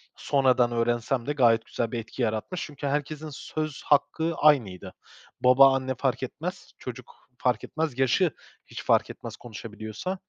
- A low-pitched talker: Yes, low, 130 Hz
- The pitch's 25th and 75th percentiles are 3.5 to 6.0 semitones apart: Yes, average, 3.9 semitones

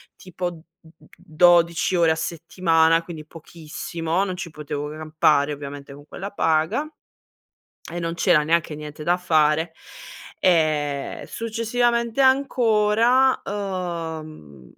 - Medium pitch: Yes, medium, 165 Hz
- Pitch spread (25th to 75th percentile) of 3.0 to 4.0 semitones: Yes, average, 3.5 semitones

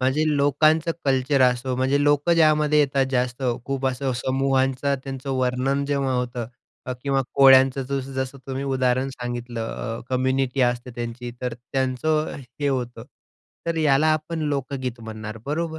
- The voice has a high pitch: No, low, 135 Hz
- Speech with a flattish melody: Yes, narrow, 2.0 semitones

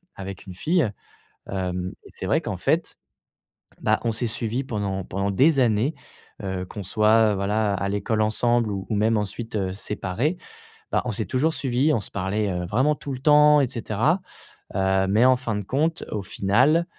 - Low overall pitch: Yes, low, 110 Hz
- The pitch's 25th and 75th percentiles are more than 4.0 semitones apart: Yes, average, 4.7 semitones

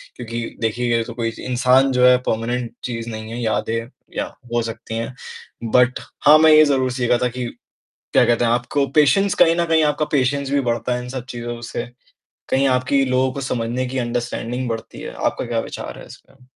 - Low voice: Yes, low, 125 Hz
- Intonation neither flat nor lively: No, narrow, 2.2 semitones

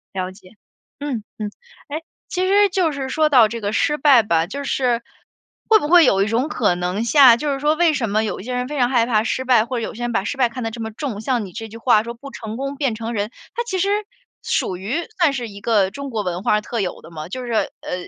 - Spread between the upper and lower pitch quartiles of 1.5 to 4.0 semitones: No, average, 4.9 semitones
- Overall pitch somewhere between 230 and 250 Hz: Yes, high, 235 Hz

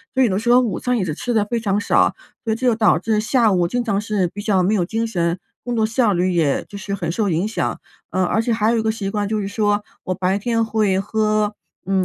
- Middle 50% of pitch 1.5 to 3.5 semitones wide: Yes, average, 2.8 semitones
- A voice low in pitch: No, high, 210 Hz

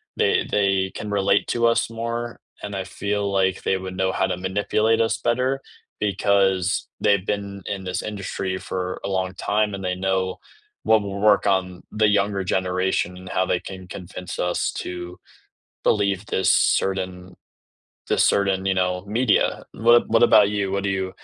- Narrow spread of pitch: Yes, narrow, 1.9 semitones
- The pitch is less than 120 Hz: Yes, very low, 95 Hz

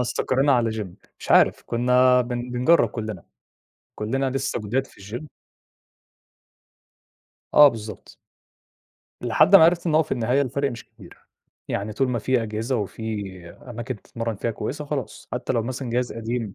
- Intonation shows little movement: No, average, 3.1 semitones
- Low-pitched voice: Yes, low, 120 Hz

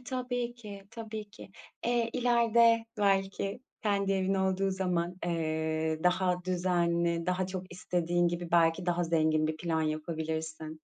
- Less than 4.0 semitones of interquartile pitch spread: Yes, average, 3.3 semitones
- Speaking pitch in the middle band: Yes, medium, 180 Hz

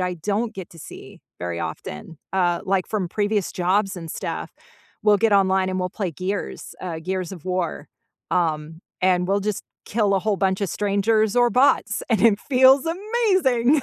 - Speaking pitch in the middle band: No, high, 195 Hz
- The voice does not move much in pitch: No, average, 3.4 semitones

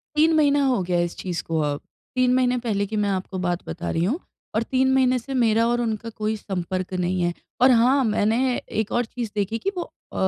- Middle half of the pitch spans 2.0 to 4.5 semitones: No, average, 5.3 semitones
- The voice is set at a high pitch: Yes, high, 225 Hz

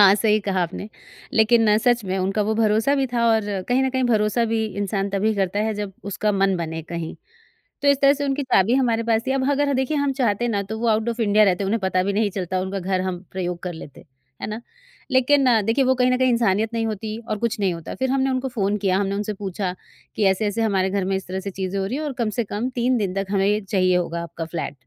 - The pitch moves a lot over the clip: No, average, 3.7 semitones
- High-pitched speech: Yes, high, 210 Hz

